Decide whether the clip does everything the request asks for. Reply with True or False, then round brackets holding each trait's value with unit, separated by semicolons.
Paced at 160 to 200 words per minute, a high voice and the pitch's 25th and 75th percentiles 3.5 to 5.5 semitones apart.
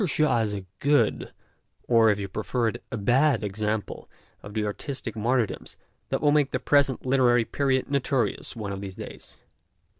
False (170 wpm; 120 Hz; 4.4 semitones)